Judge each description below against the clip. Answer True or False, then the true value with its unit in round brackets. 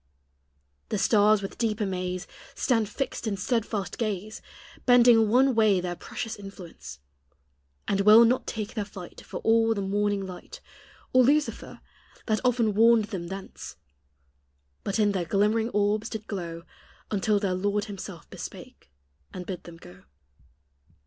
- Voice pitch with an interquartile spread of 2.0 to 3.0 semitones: True (2.7 semitones)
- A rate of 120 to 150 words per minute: True (140 wpm)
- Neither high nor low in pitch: False (205 Hz)